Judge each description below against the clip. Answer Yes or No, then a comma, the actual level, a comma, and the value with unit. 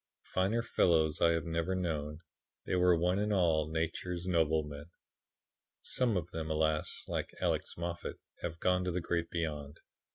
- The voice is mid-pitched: No, very low, 85 Hz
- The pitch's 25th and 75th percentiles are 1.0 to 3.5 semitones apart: Yes, narrow, 2.4 semitones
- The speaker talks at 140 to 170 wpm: Yes, average, 155 wpm